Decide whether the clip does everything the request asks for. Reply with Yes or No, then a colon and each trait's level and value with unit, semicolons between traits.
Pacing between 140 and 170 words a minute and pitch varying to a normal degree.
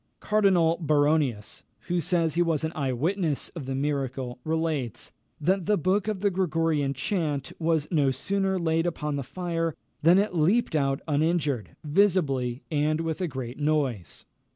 Yes: average, 155 wpm; average, 3.9 semitones